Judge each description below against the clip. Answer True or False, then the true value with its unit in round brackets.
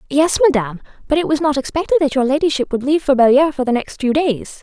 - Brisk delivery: True (245 wpm)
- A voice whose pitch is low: False (280 Hz)